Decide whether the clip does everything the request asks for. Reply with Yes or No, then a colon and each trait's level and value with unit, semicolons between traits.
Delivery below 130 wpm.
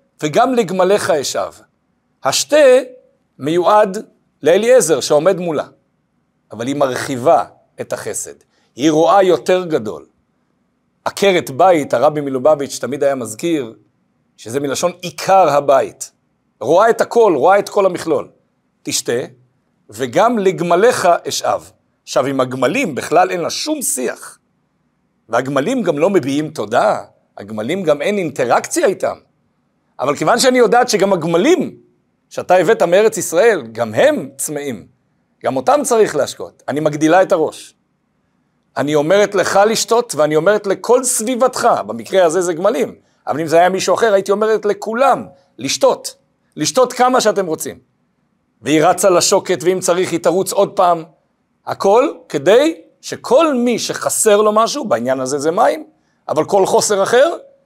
No: average, 135 wpm